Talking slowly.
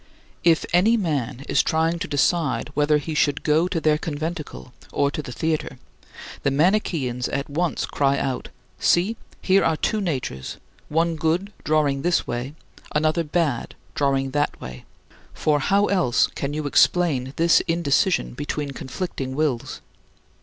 No: average, 150 wpm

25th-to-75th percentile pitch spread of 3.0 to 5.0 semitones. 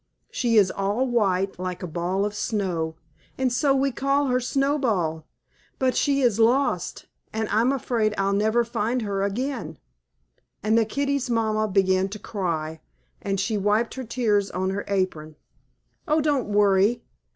Yes: average, 4.3 semitones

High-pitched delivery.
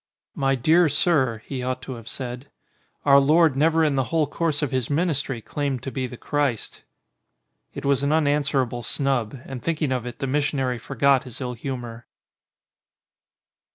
No: low, 135 Hz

